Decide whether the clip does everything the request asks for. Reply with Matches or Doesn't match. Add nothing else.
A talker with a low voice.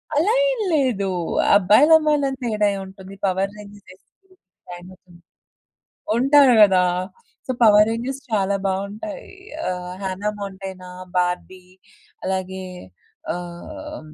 Doesn't match